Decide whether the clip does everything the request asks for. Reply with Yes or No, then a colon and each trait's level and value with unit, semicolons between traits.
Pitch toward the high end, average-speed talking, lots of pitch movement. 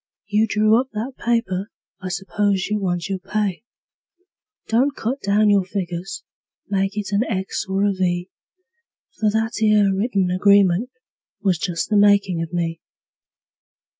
No: high, 200 Hz; average, 145 wpm; narrow, 2.4 semitones